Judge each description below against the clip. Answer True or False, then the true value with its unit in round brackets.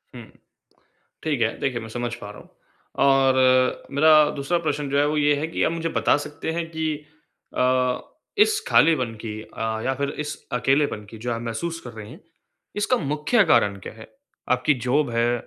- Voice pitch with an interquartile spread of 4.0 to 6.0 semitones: True (4.4 semitones)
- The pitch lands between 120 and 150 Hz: True (135 Hz)